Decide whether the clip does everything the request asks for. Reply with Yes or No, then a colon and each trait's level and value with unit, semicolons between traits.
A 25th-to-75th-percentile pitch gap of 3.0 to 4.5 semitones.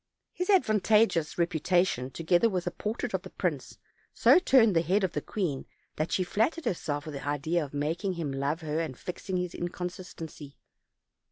Yes: average, 4.2 semitones